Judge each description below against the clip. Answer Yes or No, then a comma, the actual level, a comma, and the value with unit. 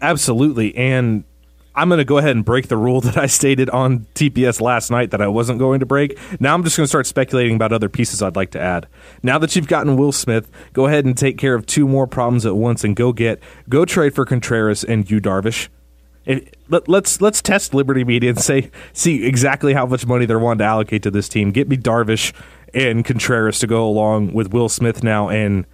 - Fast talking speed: Yes, fast, 225 wpm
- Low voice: Yes, low, 125 Hz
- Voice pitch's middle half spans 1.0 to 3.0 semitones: No, average, 3.8 semitones